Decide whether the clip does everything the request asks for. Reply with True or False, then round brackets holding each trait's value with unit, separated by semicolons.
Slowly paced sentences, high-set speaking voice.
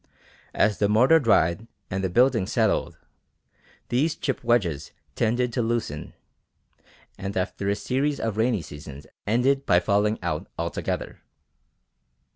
False (125 wpm; 110 Hz)